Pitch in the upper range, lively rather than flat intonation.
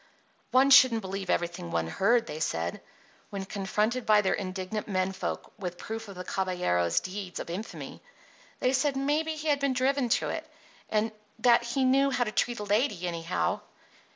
Yes: high, 215 Hz; wide, 5.7 semitones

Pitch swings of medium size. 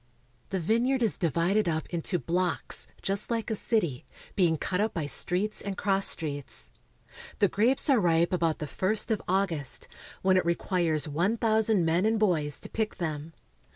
Yes: average, 4.5 semitones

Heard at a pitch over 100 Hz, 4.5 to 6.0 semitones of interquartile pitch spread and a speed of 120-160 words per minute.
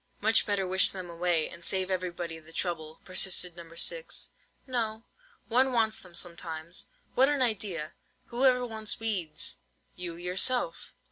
Yes: medium, 185 Hz; average, 4.8 semitones; average, 145 wpm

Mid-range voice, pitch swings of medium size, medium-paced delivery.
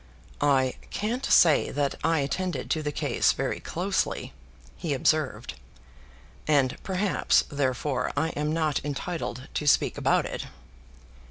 No: medium, 150 Hz; average, 3.3 semitones; slow, 125 wpm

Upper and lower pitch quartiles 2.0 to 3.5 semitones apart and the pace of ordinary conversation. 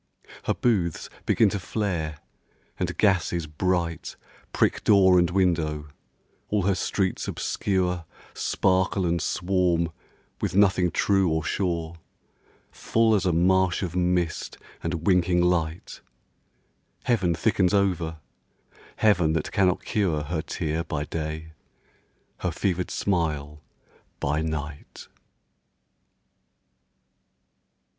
No: average, 2.8 semitones; slow, 105 wpm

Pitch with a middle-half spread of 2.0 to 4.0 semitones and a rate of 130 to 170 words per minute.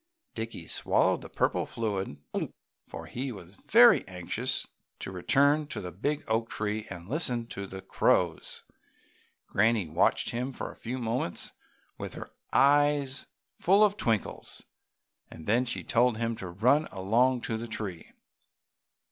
No: average, 5.2 semitones; average, 140 wpm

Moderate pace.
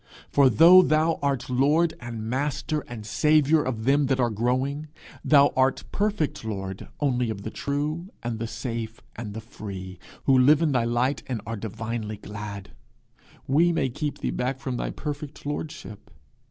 Yes: average, 165 wpm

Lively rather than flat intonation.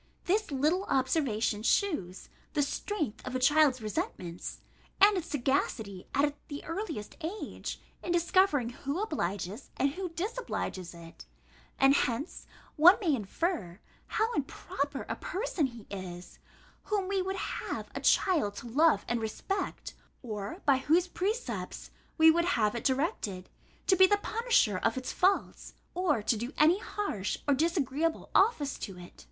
Yes: wide, 8.4 semitones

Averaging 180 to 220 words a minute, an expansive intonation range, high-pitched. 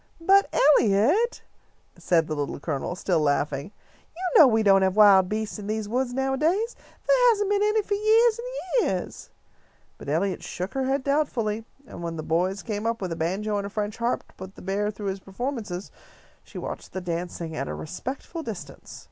Yes: average, 190 wpm; wide, 7.8 semitones; high, 210 Hz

